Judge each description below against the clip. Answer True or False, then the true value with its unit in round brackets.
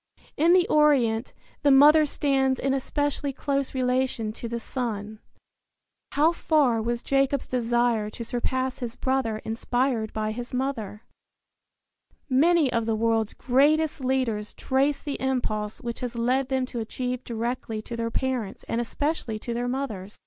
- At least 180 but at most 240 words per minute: False (150 wpm)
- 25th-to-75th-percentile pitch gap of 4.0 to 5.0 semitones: False (3.1 semitones)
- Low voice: False (250 Hz)